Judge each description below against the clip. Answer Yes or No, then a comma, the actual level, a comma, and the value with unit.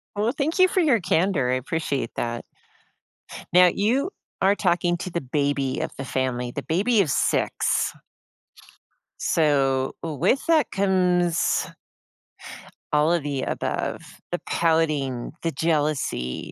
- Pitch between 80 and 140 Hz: No, medium, 165 Hz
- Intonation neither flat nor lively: No, wide, 5.8 semitones